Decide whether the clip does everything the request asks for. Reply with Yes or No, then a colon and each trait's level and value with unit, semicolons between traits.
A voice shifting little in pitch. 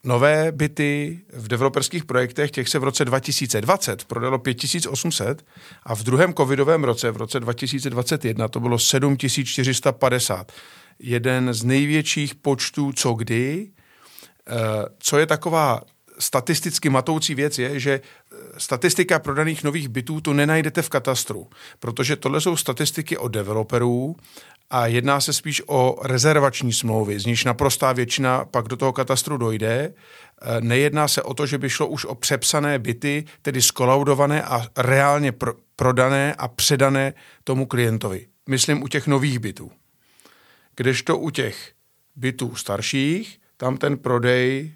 No: average, 3.1 semitones